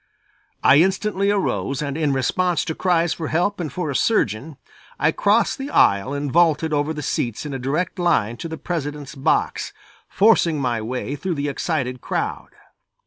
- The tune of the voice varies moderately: Yes, average, 4.4 semitones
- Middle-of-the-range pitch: Yes, medium, 155 Hz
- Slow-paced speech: No, average, 175 wpm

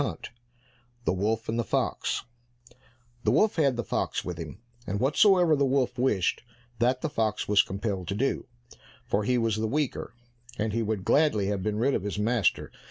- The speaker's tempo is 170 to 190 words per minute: Yes, average, 185 wpm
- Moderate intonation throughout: Yes, average, 4.4 semitones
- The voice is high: No, low, 115 Hz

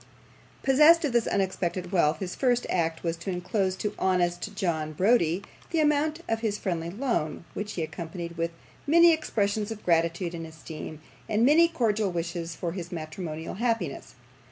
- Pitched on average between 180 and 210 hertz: Yes, medium, 185 Hz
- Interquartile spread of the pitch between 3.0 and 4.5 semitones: No, average, 5.3 semitones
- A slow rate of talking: No, average, 160 wpm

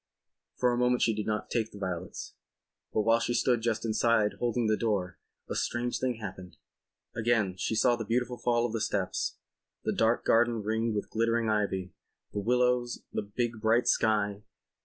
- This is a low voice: Yes, low, 115 Hz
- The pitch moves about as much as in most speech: No, narrow, 2.3 semitones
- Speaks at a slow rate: No, average, 180 wpm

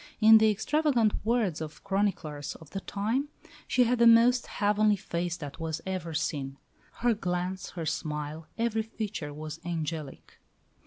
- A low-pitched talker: No, high, 190 Hz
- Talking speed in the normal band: Yes, average, 150 wpm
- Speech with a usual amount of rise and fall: No, wide, 5.9 semitones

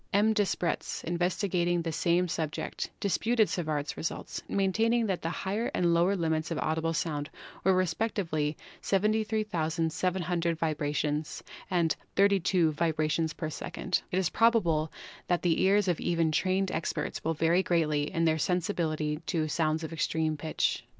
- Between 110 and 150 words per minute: Yes, average, 145 wpm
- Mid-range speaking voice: Yes, medium, 170 Hz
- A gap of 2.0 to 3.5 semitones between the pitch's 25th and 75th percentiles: Yes, average, 3.2 semitones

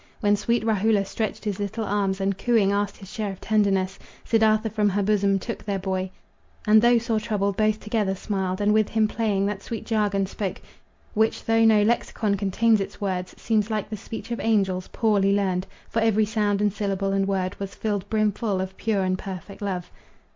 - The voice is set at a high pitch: Yes, high, 205 Hz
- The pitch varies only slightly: Yes, narrow, 1.9 semitones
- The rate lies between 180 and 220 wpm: Yes, average, 195 wpm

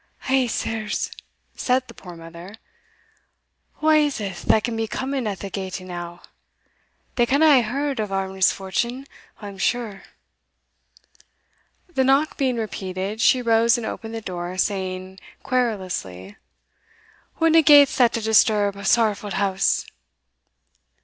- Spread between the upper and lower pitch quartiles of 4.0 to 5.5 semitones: Yes, average, 4.9 semitones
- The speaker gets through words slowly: Yes, slow, 130 wpm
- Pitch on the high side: Yes, high, 220 Hz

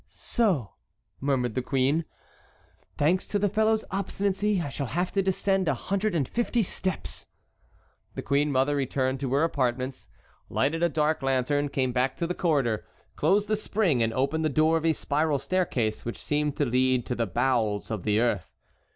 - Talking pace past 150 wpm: Yes, average, 175 wpm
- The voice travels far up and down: Yes, wide, 5.8 semitones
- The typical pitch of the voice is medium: Yes, medium, 145 Hz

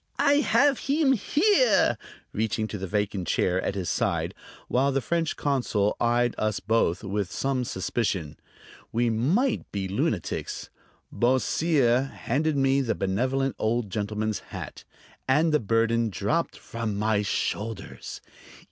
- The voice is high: No, low, 115 Hz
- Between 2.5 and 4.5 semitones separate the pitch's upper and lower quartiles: No, average, 5.0 semitones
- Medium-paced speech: No, slow, 130 wpm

